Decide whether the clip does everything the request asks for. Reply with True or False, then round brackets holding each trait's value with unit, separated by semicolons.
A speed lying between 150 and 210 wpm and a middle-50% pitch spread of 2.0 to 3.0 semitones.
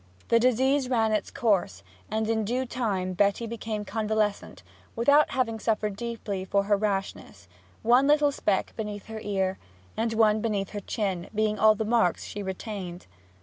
True (160 wpm; 2.6 semitones)